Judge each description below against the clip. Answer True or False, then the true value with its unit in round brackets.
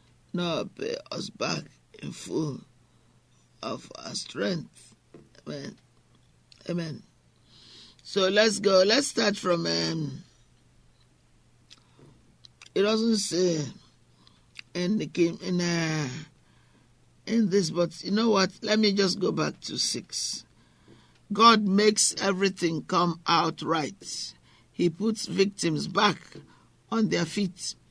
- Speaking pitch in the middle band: True (180 Hz)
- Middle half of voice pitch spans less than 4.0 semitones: False (5.3 semitones)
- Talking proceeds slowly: True (110 wpm)